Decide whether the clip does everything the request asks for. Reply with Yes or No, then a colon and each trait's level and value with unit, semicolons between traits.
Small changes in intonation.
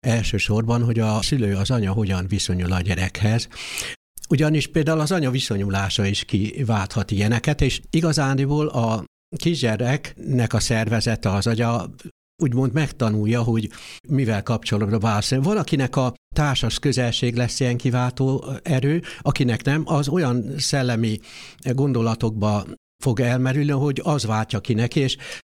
No: average, 4.1 semitones